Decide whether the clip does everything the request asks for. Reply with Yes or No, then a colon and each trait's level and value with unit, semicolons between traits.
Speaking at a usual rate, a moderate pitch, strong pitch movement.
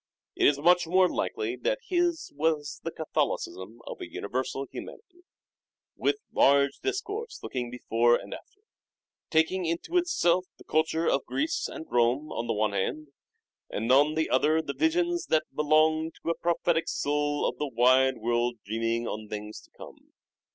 Yes: average, 165 wpm; medium, 155 Hz; wide, 6.5 semitones